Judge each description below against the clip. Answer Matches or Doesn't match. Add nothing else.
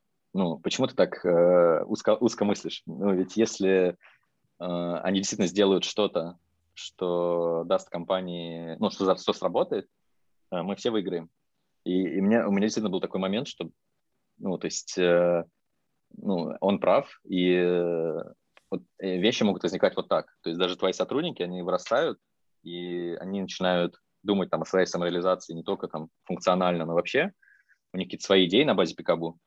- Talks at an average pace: Doesn't match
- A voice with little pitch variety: Matches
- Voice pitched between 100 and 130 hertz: Doesn't match